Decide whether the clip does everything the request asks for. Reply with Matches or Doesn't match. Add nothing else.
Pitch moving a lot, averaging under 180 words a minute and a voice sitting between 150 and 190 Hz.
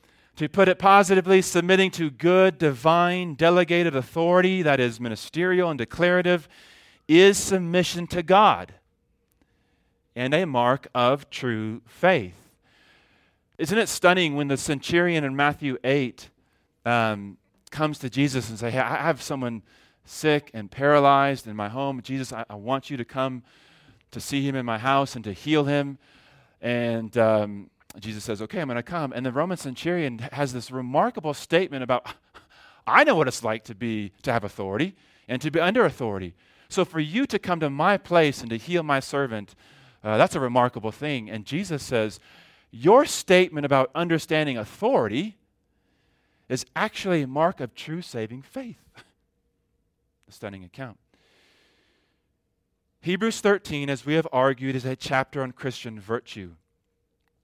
Doesn't match